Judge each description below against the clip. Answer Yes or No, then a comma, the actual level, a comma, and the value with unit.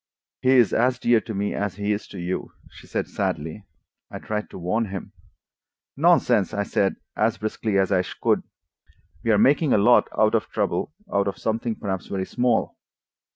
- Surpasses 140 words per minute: Yes, average, 180 wpm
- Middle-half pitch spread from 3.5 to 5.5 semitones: No, average, 2.8 semitones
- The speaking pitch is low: Yes, low, 105 Hz